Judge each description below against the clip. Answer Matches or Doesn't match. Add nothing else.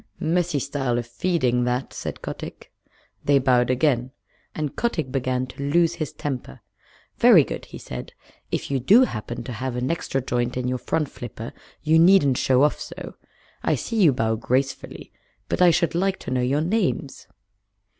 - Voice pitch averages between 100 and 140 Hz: Matches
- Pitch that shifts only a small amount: Doesn't match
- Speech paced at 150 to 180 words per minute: Matches